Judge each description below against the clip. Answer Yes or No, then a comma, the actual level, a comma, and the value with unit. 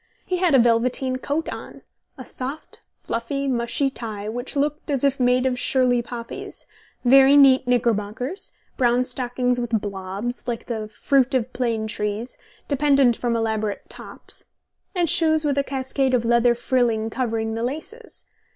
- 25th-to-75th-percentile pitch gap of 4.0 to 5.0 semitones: No, average, 2.9 semitones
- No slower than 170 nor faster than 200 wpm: No, average, 150 wpm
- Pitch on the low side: No, high, 245 Hz